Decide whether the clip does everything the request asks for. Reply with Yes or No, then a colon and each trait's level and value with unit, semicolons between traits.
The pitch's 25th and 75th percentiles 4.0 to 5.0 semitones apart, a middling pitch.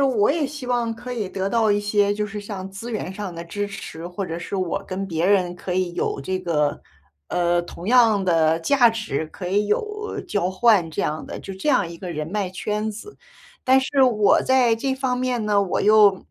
No: average, 4.5 semitones; high, 205 Hz